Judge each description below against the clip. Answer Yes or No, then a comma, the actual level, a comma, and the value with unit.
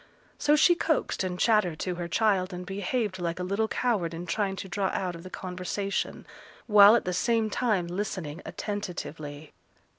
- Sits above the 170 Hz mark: Yes, high, 190 Hz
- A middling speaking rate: Yes, average, 175 wpm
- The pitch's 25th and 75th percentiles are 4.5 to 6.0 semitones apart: No, average, 3.1 semitones